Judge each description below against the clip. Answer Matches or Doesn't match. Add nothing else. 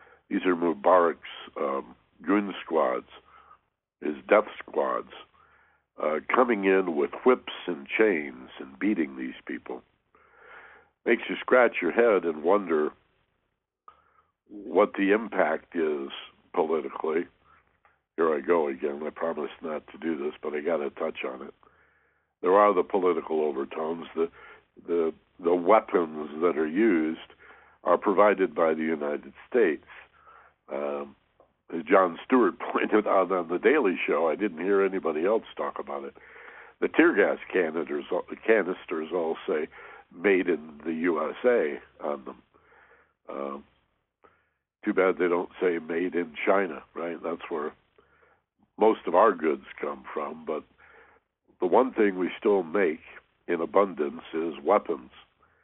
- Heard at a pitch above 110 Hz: Doesn't match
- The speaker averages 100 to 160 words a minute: Matches